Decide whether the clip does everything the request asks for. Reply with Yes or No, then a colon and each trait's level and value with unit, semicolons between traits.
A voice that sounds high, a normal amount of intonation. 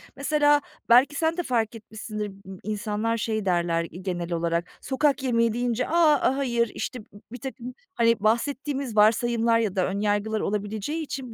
Yes: high, 230 Hz; average, 4.2 semitones